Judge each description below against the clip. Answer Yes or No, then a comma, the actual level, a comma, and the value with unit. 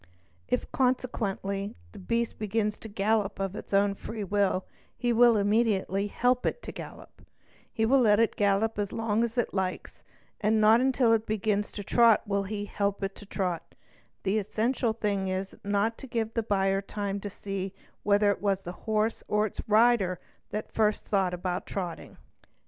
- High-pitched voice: Yes, high, 205 Hz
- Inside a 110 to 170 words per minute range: No, average, 185 wpm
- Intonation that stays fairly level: Yes, narrow, 2.2 semitones